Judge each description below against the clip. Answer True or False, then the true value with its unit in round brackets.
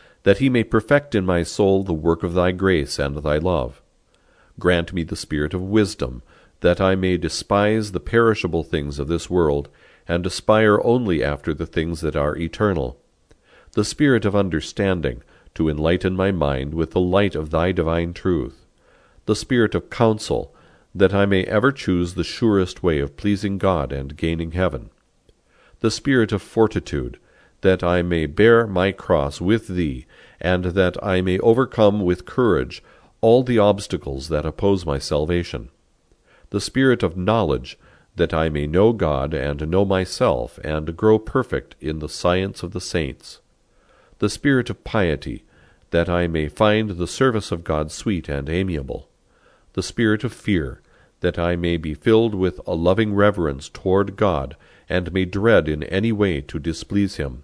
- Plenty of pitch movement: False (4.2 semitones)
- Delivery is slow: False (165 wpm)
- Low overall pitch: True (90 Hz)